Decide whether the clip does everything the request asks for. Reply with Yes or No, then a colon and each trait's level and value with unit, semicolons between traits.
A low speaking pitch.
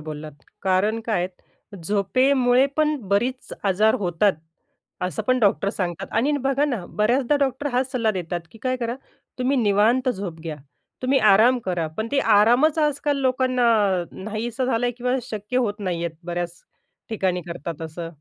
No: high, 220 Hz